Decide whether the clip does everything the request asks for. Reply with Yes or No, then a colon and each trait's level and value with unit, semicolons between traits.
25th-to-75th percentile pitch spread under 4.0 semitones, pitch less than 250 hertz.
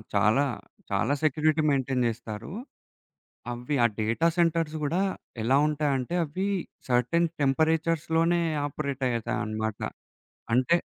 No: average, 4.7 semitones; medium, 140 Hz